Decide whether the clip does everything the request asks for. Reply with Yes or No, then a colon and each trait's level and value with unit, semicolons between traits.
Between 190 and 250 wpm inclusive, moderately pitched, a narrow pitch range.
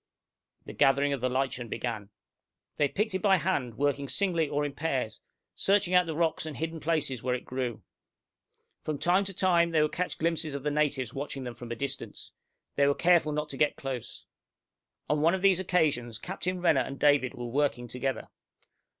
No: average, 195 wpm; medium, 145 Hz; average, 4.4 semitones